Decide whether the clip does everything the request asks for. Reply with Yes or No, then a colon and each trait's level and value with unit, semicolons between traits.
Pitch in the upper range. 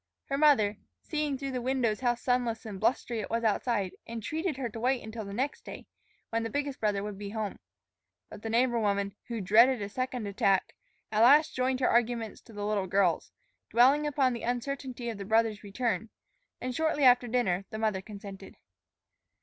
Yes: high, 230 Hz